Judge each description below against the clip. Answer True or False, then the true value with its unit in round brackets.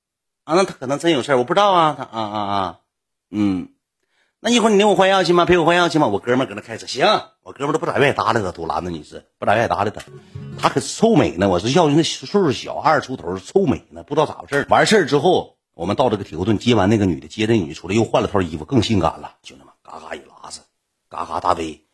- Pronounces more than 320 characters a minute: True (385 characters per minute)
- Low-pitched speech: True (120 Hz)